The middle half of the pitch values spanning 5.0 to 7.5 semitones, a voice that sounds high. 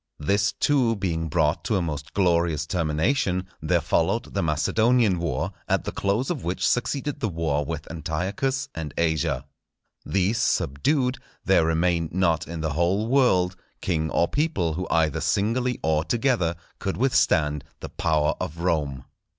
No: wide, 5.6 semitones; very low, 85 Hz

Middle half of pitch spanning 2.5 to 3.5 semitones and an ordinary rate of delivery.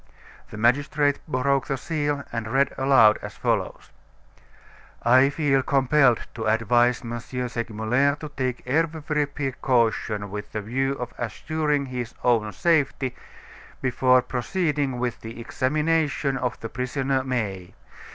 No: average, 3.2 semitones; slow, 125 wpm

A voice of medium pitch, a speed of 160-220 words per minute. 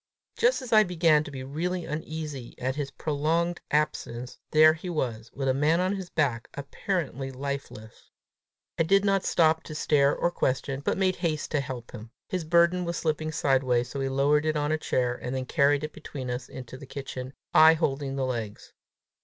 Yes: medium, 150 Hz; average, 195 wpm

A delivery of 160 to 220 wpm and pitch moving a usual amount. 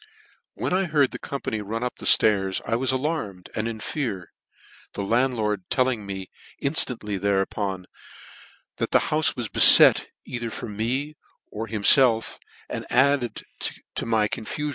No: average, 140 wpm; average, 4.3 semitones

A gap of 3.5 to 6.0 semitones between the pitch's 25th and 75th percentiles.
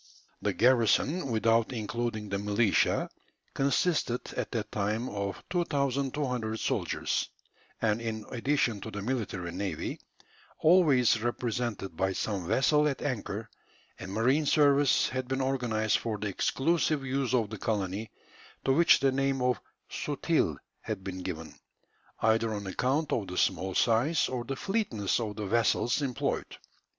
Yes: average, 4.4 semitones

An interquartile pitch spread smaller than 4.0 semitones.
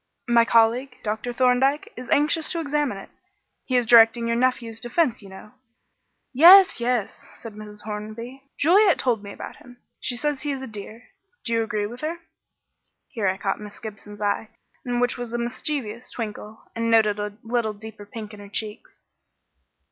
Yes: average, 3.0 semitones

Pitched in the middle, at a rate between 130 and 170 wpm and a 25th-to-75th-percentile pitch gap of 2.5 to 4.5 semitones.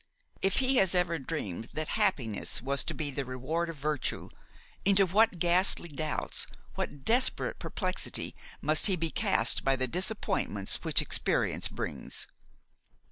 No: medium, 160 Hz; average, 140 wpm; wide, 5.6 semitones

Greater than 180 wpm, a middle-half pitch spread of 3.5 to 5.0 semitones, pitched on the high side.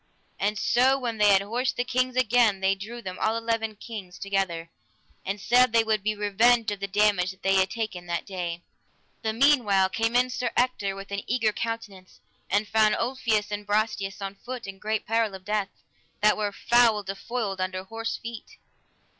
No: average, 190 wpm; average, 2.9 semitones; high, 210 Hz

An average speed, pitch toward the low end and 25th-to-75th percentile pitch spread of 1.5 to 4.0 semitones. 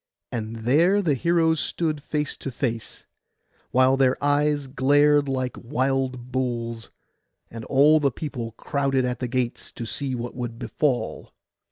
Yes: average, 145 wpm; low, 130 Hz; average, 3.1 semitones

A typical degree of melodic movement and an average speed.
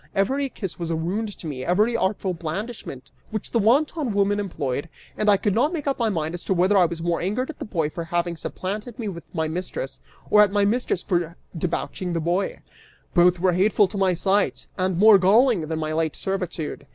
No: average, 3.8 semitones; fast, 215 wpm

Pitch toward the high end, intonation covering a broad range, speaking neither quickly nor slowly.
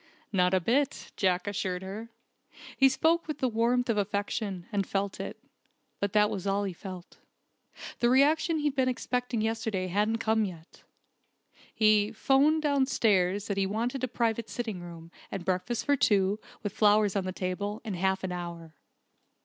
No: high, 210 Hz; average, 4.2 semitones; average, 165 wpm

